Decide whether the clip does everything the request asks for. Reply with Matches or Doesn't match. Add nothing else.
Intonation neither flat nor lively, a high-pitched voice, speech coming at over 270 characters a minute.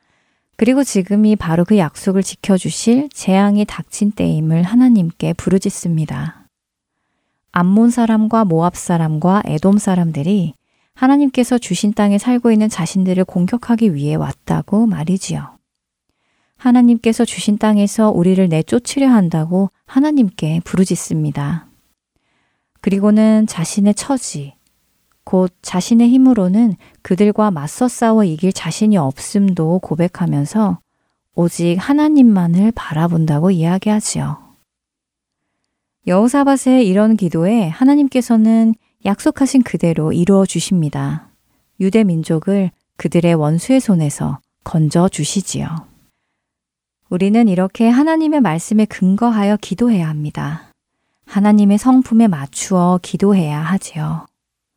Matches